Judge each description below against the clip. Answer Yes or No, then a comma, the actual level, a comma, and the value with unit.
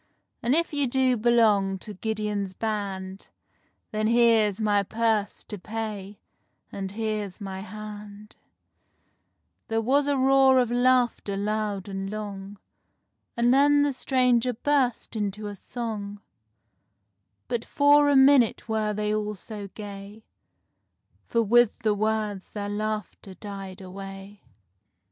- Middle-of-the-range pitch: No, high, 215 Hz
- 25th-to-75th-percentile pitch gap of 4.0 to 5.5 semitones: No, average, 2.9 semitones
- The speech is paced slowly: Yes, slow, 120 wpm